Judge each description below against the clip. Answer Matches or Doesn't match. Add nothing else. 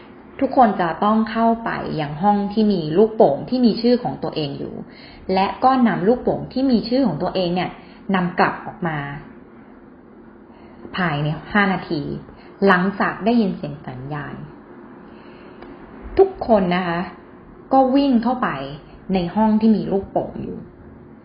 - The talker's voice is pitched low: Doesn't match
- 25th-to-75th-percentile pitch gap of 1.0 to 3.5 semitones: Doesn't match